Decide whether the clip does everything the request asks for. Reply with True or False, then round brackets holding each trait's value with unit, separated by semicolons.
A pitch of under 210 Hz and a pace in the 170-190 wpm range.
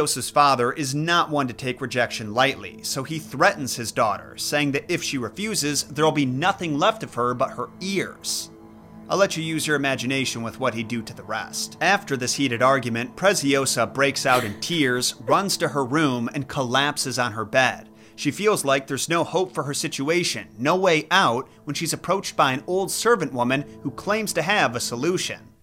False (140 Hz; 200 wpm)